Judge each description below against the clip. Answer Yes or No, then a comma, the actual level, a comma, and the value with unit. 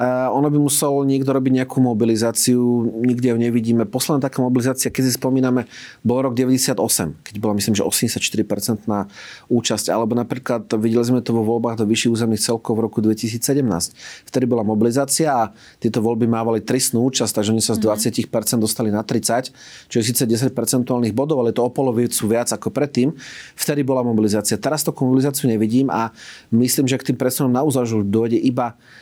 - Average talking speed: No, fast, 180 wpm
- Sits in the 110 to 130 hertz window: Yes, low, 120 Hz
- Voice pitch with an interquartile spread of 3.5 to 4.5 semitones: No, narrow, 2.4 semitones